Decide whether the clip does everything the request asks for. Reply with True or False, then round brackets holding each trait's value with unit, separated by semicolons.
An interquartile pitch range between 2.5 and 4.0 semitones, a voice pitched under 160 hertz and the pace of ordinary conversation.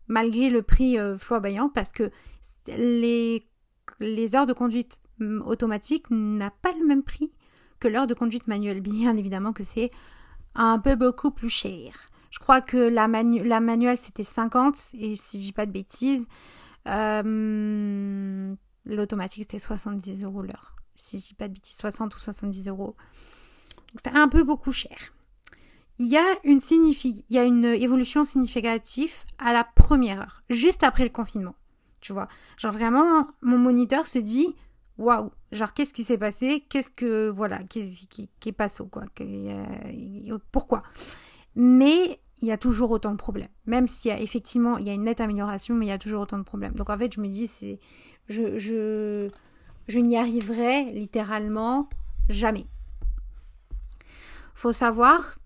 False (2.9 semitones; 230 Hz; 170 wpm)